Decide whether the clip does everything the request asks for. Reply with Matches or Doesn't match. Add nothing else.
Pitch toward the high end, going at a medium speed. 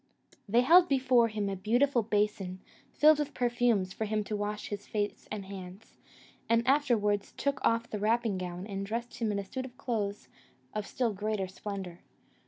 Matches